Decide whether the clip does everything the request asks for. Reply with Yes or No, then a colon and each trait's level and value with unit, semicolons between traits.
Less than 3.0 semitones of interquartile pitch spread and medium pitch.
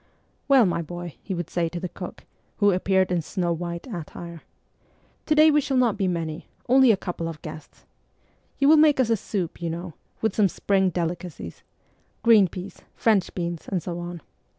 No: average, 4.3 semitones; medium, 180 Hz